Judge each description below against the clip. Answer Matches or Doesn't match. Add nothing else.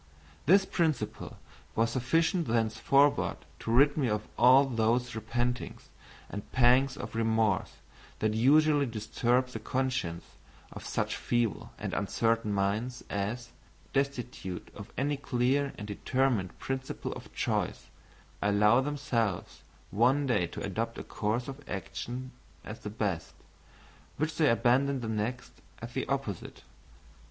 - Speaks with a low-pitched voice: Matches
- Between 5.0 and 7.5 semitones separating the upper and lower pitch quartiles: Doesn't match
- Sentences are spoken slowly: Matches